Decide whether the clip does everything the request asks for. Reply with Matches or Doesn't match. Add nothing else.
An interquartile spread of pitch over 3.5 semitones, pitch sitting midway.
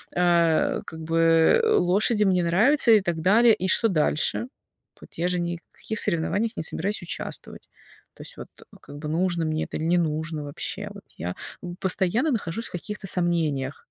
Matches